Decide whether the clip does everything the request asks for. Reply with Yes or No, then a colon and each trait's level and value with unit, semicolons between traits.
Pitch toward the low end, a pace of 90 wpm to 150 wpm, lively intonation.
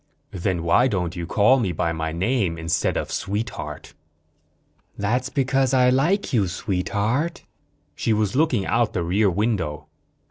Yes: low, 105 Hz; average, 145 wpm; wide, 6.3 semitones